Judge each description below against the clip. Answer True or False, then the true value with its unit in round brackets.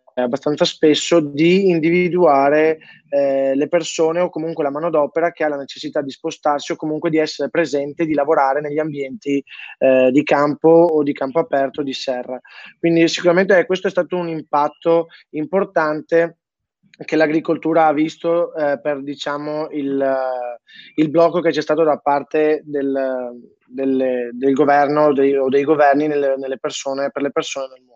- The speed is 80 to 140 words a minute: False (165 wpm)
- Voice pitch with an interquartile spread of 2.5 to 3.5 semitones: True (2.9 semitones)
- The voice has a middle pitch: True (150 Hz)